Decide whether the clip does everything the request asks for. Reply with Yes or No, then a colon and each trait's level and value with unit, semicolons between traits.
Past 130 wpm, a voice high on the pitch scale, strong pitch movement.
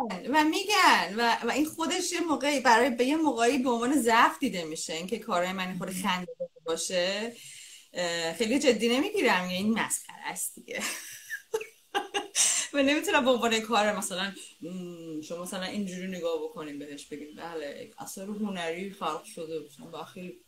Yes: average, 150 wpm; high, 220 Hz; wide, 8.1 semitones